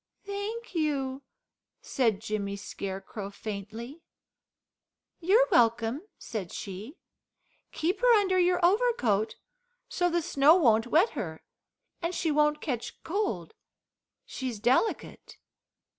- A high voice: Yes, very high, 275 Hz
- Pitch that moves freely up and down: Yes, wide, 8.7 semitones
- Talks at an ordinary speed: No, slow, 105 wpm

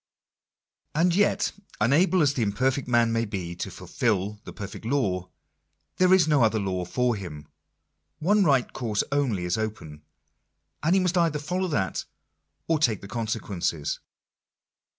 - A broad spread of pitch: Yes, wide, 7.4 semitones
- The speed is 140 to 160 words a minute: Yes, average, 150 wpm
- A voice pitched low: Yes, low, 115 Hz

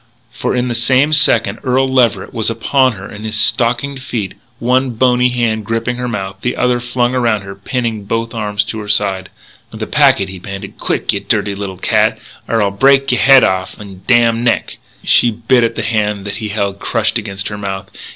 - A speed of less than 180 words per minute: No, average, 200 wpm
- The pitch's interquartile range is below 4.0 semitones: Yes, average, 3.5 semitones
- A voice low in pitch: Yes, low, 115 Hz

